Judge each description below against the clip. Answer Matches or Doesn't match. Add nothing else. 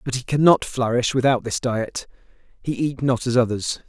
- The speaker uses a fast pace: Doesn't match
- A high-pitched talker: Doesn't match